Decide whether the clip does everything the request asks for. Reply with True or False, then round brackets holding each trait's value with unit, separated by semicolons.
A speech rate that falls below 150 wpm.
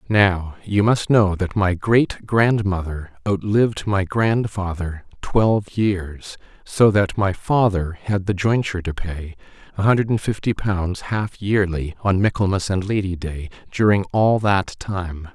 True (140 wpm)